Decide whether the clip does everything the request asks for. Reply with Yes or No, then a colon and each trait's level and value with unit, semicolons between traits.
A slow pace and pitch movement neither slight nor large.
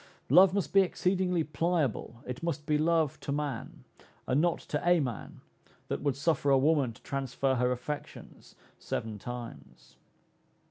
No: average, 150 wpm; average, 4.7 semitones